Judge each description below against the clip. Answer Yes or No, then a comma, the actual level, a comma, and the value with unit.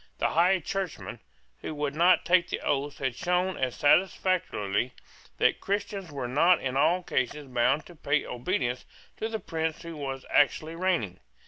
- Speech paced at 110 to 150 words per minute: No, average, 160 wpm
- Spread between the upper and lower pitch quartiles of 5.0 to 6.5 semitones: Yes, average, 5.3 semitones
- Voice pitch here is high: No, medium, 155 Hz